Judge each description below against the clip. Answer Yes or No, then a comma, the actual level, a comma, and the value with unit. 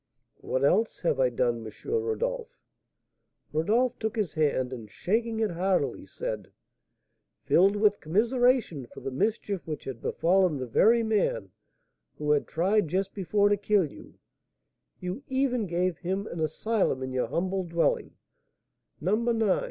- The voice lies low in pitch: No, high, 190 Hz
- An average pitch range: No, wide, 6.3 semitones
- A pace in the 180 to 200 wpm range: No, average, 145 wpm